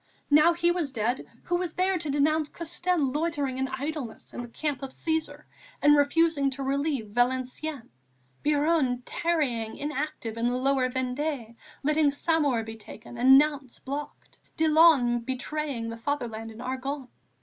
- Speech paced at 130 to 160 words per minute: Yes, average, 150 wpm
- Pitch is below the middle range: No, very high, 280 Hz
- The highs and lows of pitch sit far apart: No, average, 3.6 semitones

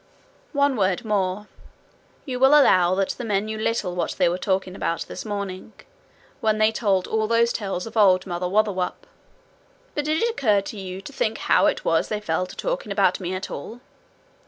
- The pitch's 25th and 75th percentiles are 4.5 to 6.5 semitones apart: No, average, 3.5 semitones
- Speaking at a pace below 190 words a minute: No, average, 195 wpm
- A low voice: No, high, 205 Hz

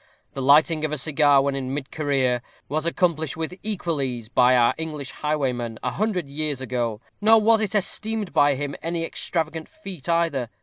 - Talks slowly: No, average, 180 wpm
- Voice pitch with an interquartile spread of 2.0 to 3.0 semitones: No, average, 4.1 semitones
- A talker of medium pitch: Yes, medium, 150 Hz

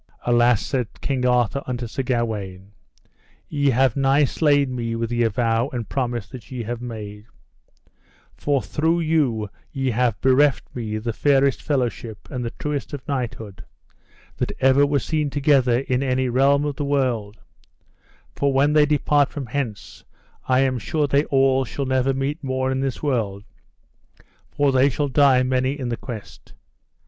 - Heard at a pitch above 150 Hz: No, low, 130 Hz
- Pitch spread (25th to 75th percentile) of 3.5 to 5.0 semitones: No, average, 2.9 semitones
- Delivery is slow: No, average, 160 wpm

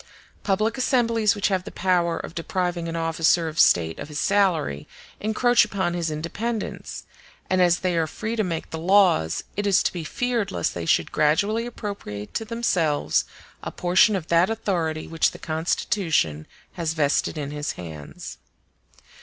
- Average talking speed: Yes, average, 165 wpm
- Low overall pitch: No, medium, 175 Hz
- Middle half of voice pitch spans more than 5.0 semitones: No, average, 4.6 semitones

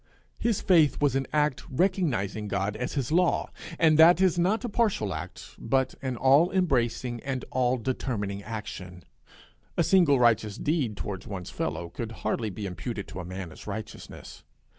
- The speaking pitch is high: No, low, 125 Hz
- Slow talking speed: No, average, 165 wpm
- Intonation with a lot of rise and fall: Yes, wide, 7.4 semitones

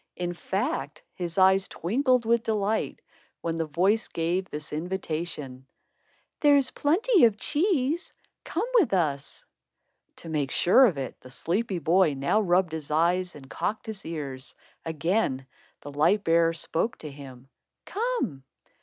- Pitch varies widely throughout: Yes, wide, 6.4 semitones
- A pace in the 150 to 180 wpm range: No, average, 140 wpm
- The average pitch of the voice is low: No, medium, 175 Hz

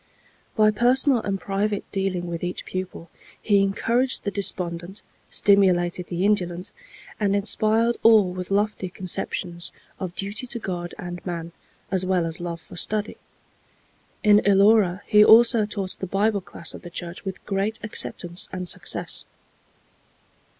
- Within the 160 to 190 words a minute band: No, average, 145 wpm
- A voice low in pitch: No, high, 195 Hz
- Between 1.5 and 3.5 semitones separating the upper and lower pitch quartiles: Yes, average, 2.9 semitones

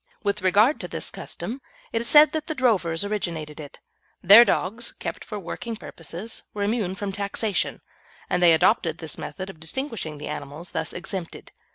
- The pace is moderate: Yes, average, 175 wpm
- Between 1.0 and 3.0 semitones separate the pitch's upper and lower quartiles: No, average, 5.3 semitones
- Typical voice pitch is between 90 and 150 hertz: No, high, 195 Hz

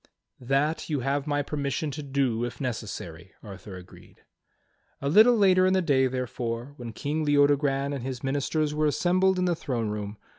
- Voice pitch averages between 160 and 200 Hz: No, medium, 140 Hz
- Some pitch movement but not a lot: Yes, average, 3.9 semitones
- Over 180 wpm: No, average, 175 wpm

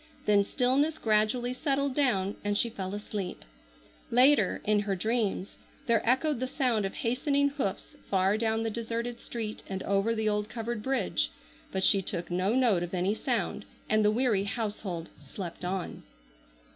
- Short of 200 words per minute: Yes, average, 160 wpm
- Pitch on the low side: No, high, 215 Hz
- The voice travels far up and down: No, average, 3.8 semitones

